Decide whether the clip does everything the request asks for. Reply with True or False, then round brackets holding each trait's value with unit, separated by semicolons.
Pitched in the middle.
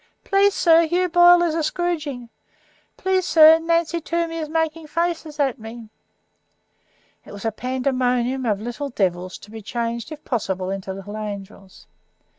False (275 Hz)